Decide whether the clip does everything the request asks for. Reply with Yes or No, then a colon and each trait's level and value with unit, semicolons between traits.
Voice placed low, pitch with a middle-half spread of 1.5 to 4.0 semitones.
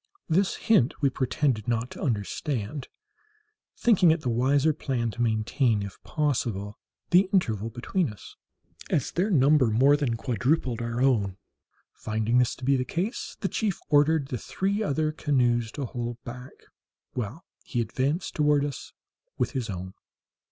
No: low, 130 Hz; average, 4.6 semitones